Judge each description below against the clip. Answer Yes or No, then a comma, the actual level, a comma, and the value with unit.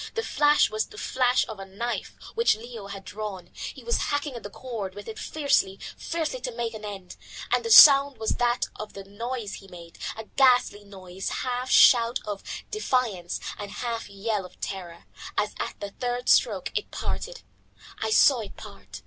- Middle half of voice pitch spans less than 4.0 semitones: No, average, 4.4 semitones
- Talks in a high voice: Yes, high, 220 Hz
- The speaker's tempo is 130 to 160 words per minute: No, average, 185 wpm